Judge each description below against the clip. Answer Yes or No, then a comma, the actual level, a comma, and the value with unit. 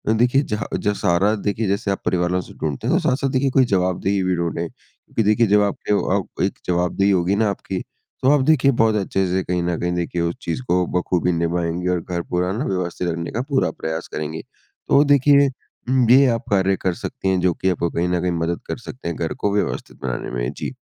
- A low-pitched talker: Yes, very low, 90 Hz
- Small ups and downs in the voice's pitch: No, average, 3.5 semitones